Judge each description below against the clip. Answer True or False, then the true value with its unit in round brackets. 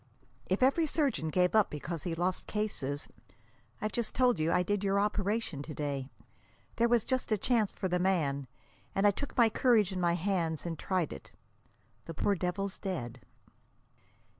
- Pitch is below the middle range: False (190 Hz)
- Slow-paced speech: False (175 wpm)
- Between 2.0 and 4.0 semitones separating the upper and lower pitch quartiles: False (4.6 semitones)